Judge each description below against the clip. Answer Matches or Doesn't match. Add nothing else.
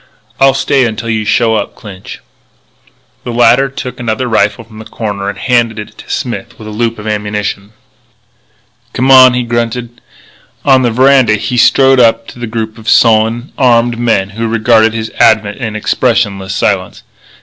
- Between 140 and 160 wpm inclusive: Doesn't match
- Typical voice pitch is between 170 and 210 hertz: Doesn't match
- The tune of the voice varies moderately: Doesn't match